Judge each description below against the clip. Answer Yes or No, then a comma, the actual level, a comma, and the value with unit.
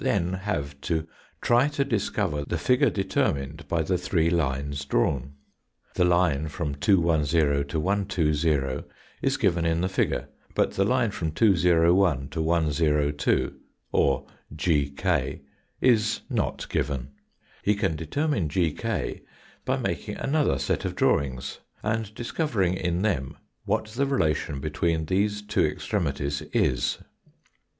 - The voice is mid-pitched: No, very low, 85 Hz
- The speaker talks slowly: Yes, slow, 130 wpm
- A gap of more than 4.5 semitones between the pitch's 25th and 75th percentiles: Yes, wide, 5.5 semitones